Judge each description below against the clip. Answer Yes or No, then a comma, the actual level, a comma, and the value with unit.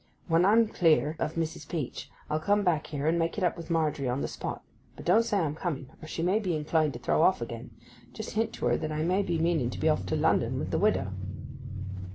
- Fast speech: Yes, fast, 245 wpm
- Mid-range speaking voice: Yes, medium, 160 Hz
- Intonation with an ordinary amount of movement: Yes, average, 3.2 semitones